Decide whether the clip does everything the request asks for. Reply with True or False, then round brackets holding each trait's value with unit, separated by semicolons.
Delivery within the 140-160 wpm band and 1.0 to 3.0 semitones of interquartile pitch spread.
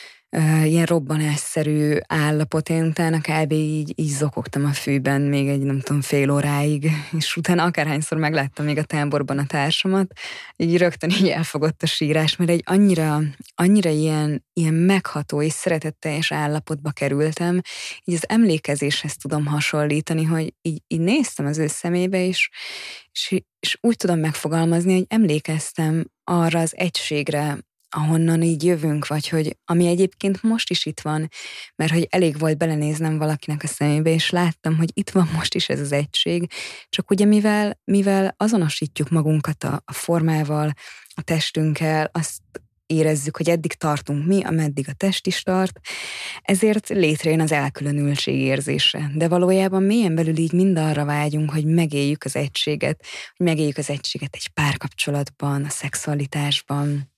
True (150 wpm; 2.6 semitones)